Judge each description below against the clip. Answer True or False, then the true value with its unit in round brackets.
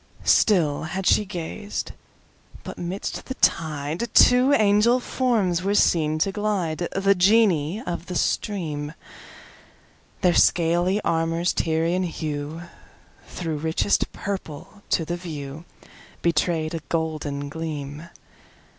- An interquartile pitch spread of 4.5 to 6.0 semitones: False (3.9 semitones)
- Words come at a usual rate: False (95 wpm)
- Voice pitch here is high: False (170 Hz)